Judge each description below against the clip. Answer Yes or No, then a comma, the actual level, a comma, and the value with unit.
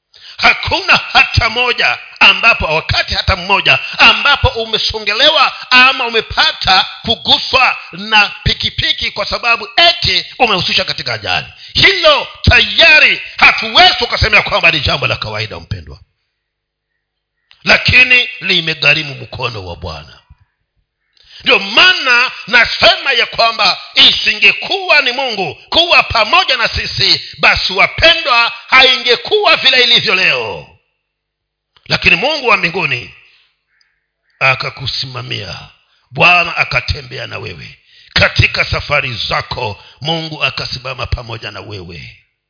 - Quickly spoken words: No, slow, 100 wpm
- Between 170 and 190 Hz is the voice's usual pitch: Yes, medium, 185 Hz